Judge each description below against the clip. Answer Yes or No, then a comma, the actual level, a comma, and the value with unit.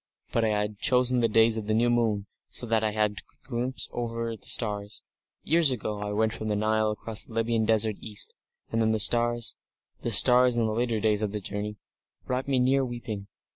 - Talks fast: Yes, fast, 215 wpm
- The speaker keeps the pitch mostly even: Yes, narrow, 2.0 semitones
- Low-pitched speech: Yes, low, 110 Hz